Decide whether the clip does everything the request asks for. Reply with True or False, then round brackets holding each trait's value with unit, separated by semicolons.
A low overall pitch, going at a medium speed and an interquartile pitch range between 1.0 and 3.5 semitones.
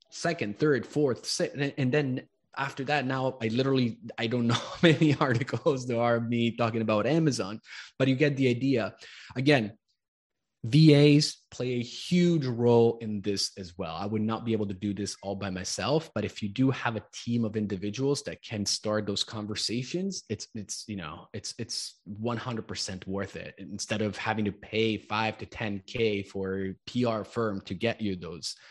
False (115 Hz; 185 wpm; 4.2 semitones)